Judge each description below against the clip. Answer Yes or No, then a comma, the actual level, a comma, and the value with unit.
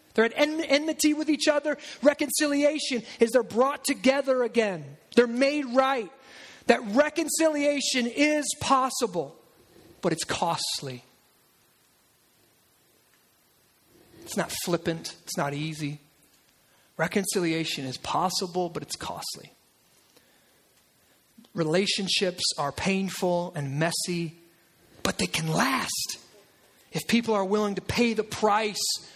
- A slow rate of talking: Yes, slow, 105 wpm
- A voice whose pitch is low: No, high, 215 Hz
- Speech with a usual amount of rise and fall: No, wide, 8.2 semitones